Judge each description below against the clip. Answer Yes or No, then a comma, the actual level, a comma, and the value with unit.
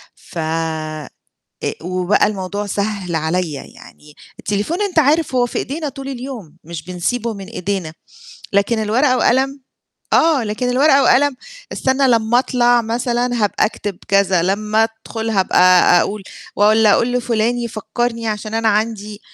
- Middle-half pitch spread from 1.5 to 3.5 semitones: No, average, 4.1 semitones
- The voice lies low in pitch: No, high, 220 Hz